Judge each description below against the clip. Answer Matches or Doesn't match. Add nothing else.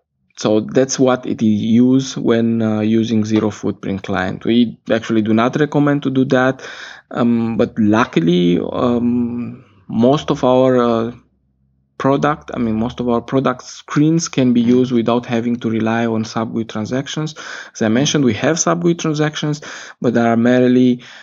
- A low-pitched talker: Matches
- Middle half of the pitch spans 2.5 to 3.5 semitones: Matches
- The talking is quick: Doesn't match